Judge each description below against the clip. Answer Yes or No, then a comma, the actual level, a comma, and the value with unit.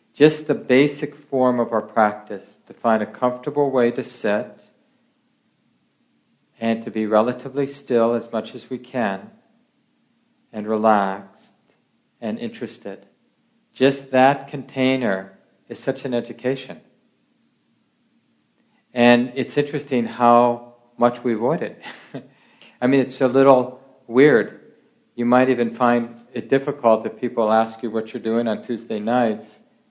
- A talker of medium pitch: No, low, 125 Hz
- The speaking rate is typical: No, slow, 130 wpm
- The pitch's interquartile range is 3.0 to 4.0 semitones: Yes, average, 3.6 semitones